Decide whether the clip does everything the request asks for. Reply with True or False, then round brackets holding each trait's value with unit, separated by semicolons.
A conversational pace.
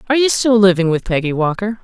False (230 wpm)